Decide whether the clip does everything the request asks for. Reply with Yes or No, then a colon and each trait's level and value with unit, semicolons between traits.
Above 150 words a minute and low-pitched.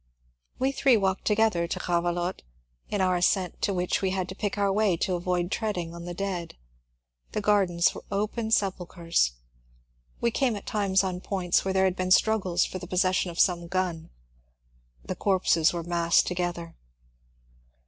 No: average, 170 wpm; medium, 185 Hz